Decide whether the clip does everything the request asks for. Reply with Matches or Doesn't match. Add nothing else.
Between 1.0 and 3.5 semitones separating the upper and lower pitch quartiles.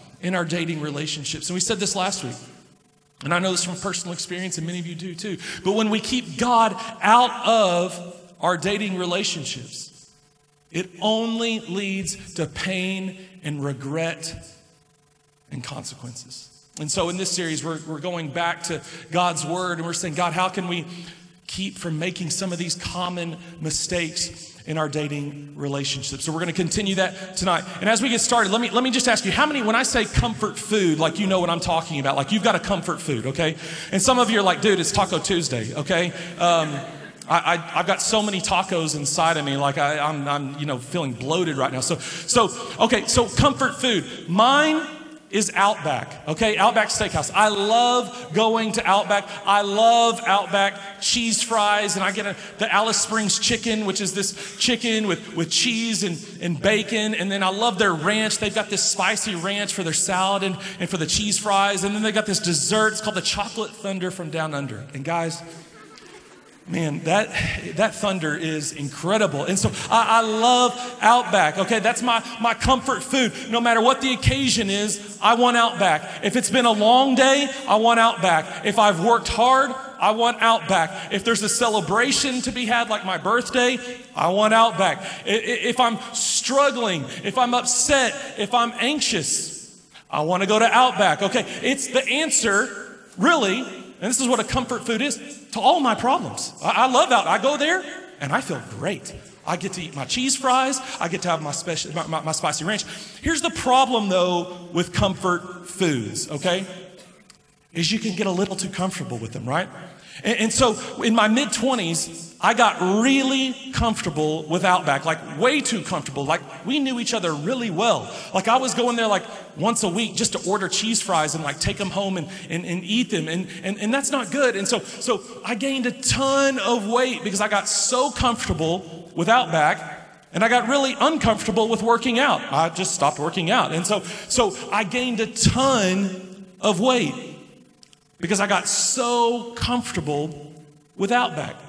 Doesn't match